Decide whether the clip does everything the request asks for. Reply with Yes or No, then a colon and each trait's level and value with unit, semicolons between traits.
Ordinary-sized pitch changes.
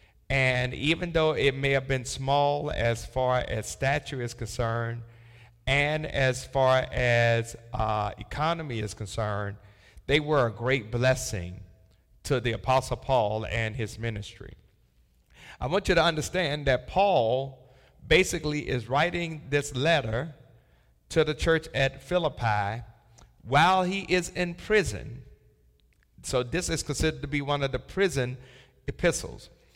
Yes: average, 4.2 semitones